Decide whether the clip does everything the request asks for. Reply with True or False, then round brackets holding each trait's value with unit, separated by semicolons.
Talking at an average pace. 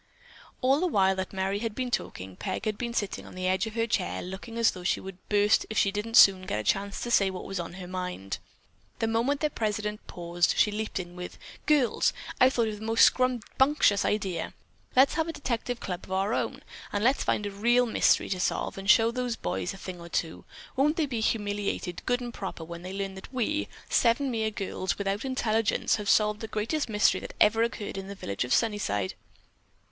False (220 wpm)